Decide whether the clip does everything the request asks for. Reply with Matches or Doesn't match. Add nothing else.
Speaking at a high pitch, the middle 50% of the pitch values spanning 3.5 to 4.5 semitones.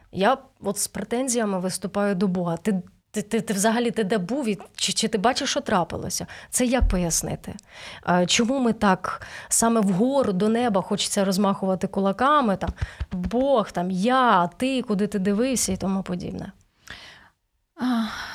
Matches